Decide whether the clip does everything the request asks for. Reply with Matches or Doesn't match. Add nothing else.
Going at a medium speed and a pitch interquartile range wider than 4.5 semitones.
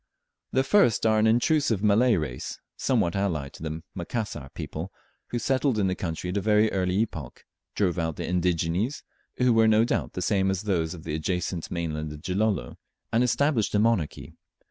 Matches